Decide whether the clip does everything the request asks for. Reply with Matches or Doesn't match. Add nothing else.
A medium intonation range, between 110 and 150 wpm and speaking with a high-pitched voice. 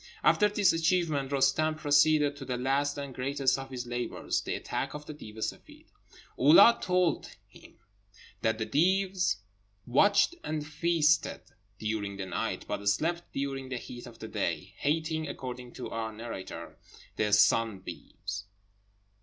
Doesn't match